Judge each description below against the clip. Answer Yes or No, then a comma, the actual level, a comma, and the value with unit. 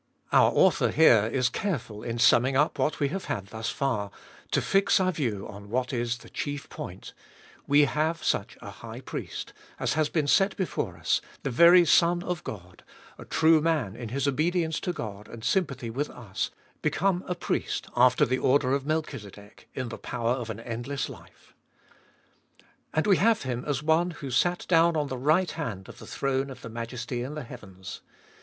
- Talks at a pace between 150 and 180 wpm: No, average, 190 wpm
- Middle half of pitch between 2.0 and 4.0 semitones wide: No, wide, 5.5 semitones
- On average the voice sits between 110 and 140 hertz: Yes, low, 135 Hz